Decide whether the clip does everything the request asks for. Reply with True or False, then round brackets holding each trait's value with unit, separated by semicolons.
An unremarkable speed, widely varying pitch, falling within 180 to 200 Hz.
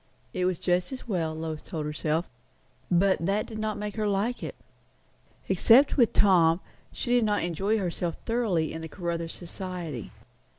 False (165 wpm; 4.2 semitones; 185 Hz)